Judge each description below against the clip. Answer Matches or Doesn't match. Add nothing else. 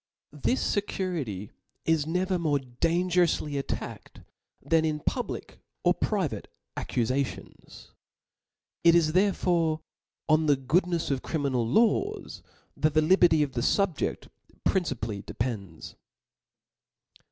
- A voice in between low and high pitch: Matches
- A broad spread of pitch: Doesn't match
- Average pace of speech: Doesn't match